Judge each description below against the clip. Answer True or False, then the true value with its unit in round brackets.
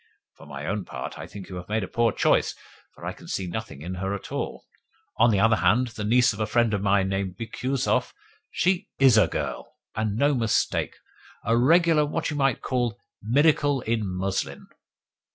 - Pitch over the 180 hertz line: False (110 Hz)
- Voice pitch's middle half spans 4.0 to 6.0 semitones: True (4.6 semitones)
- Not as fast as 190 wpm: False (195 wpm)